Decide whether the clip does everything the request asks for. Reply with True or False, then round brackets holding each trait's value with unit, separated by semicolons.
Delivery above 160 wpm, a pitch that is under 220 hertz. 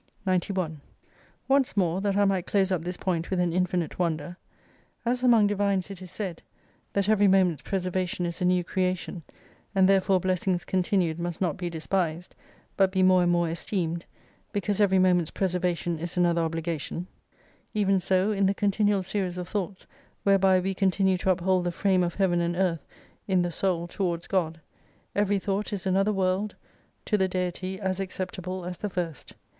True (175 wpm; 185 Hz)